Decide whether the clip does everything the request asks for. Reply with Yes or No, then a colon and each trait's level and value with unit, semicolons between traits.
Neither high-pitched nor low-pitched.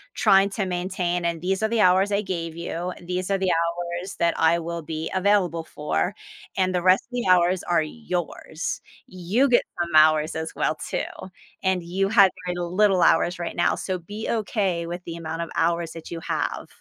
Yes: medium, 175 Hz